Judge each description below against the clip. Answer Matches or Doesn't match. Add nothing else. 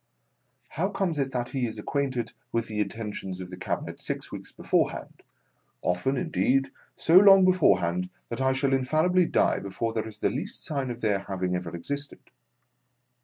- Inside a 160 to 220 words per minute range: Matches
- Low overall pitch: Matches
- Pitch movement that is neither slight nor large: Doesn't match